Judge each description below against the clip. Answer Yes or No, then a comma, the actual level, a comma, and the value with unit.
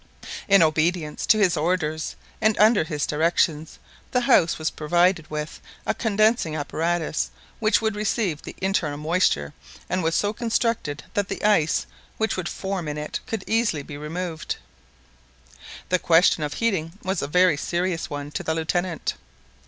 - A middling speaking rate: Yes, average, 155 wpm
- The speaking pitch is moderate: Yes, medium, 175 Hz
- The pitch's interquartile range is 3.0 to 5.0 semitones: Yes, average, 4.5 semitones